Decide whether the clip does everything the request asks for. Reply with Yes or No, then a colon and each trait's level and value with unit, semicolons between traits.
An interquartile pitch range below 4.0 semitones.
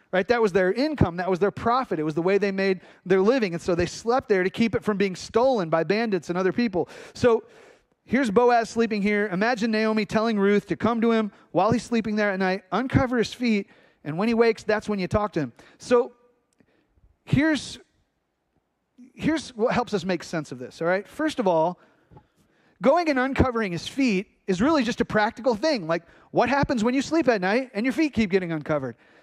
No: average, 4.4 semitones